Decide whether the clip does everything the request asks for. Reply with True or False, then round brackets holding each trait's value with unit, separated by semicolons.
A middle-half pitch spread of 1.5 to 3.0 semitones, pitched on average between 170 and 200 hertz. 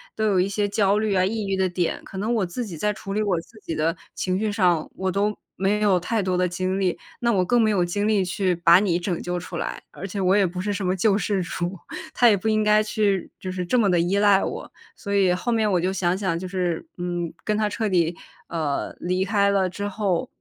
True (2.7 semitones; 190 Hz)